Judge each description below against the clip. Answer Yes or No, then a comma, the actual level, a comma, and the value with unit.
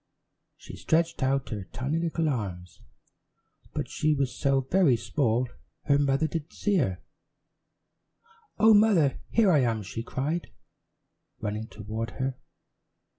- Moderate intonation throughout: No, wide, 6.1 semitones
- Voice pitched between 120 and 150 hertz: Yes, low, 135 Hz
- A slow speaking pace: Yes, slow, 125 wpm